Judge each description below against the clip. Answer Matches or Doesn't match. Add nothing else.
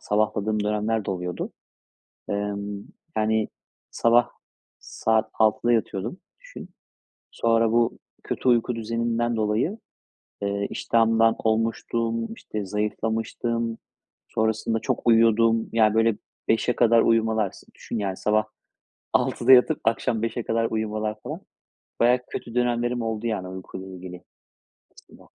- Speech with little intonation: Matches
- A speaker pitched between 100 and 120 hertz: Matches